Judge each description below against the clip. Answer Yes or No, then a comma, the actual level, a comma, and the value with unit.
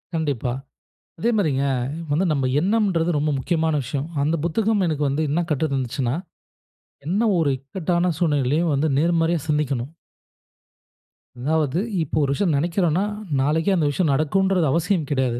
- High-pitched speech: No, medium, 160 Hz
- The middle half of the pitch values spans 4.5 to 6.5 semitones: No, average, 3.6 semitones